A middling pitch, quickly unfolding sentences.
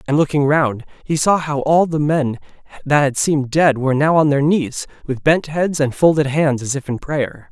Yes: medium, 145 Hz; fast, 225 wpm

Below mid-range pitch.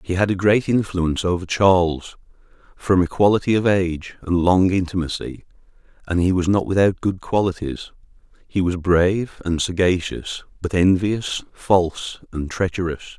Yes: very low, 90 Hz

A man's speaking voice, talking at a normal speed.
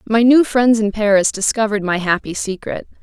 No: female; average, 180 wpm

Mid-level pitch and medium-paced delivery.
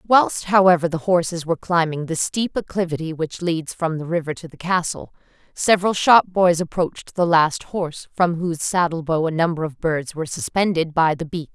Yes: medium, 170 Hz; average, 190 wpm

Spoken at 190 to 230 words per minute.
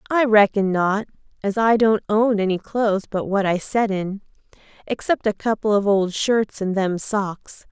No: average, 180 wpm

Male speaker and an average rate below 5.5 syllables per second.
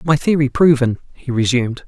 No: male; 5.6 syllables/s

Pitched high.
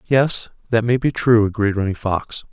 No: low, 110 Hz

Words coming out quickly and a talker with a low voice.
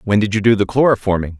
Yes: fast, 260 wpm; low, 105 Hz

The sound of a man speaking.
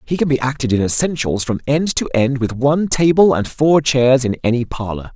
Yes: male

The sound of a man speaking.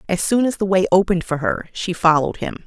No: female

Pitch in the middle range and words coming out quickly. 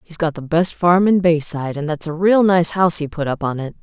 Yes: medium, 165 Hz; fast, 285 wpm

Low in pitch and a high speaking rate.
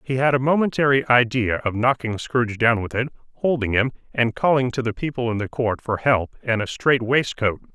Yes: low, 120 Hz; fast, 210 wpm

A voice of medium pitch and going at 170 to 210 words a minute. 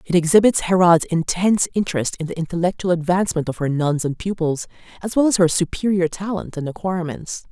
Yes: medium, 175 Hz; average, 175 wpm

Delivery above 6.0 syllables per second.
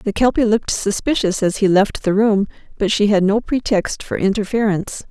No: 5.3 syllables/s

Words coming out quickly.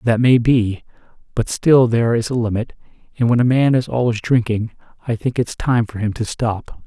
Yes: fast, 210 wpm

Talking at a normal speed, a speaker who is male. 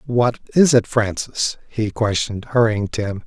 Yes: average, 165 wpm; male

